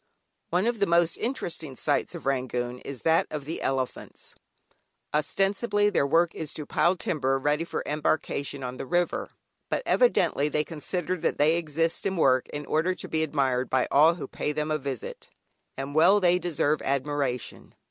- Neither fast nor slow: Yes, average, 175 wpm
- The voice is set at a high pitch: No, medium, 150 Hz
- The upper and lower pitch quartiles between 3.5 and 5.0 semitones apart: Yes, average, 3.9 semitones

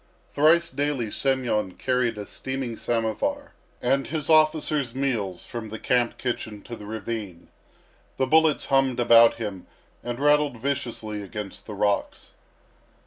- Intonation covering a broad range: No, average, 4.1 semitones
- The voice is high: No, low, 120 Hz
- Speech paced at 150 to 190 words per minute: No, slow, 135 wpm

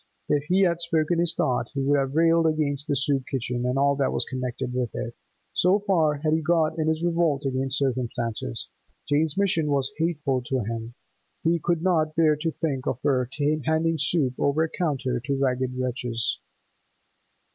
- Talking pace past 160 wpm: Yes, average, 180 wpm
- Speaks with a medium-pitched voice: Yes, medium, 145 Hz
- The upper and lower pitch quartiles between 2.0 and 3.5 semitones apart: No, average, 3.9 semitones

